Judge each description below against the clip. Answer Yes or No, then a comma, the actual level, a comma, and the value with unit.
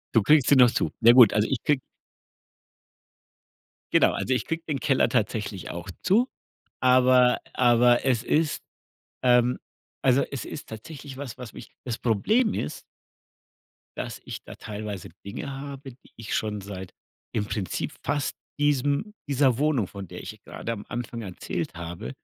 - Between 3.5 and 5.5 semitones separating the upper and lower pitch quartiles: Yes, average, 4.6 semitones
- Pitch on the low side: Yes, low, 125 Hz